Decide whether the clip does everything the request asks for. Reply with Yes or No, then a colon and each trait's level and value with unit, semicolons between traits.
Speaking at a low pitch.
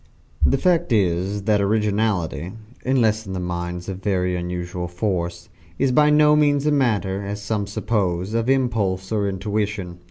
Yes: low, 100 Hz